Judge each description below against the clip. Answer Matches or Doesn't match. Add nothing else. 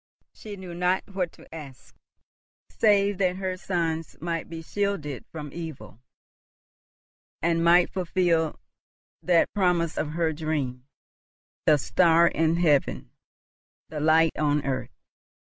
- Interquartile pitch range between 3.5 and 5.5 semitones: Doesn't match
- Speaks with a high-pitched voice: Doesn't match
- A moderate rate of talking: Doesn't match